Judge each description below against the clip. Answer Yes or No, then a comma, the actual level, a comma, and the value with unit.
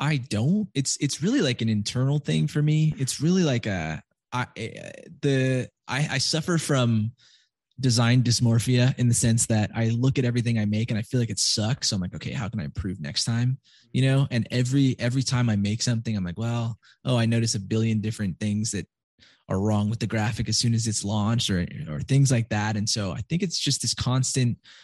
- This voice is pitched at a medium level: No, low, 120 Hz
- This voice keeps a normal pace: No, fast, 220 wpm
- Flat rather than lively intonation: No, average, 3.5 semitones